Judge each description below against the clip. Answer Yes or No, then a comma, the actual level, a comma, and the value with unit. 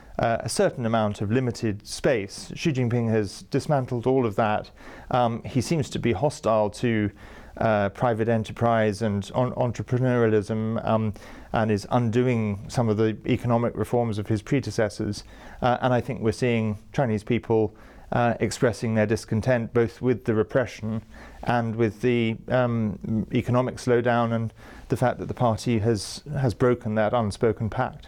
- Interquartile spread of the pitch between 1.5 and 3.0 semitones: Yes, narrow, 2.4 semitones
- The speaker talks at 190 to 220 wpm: No, average, 155 wpm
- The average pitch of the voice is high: No, low, 115 Hz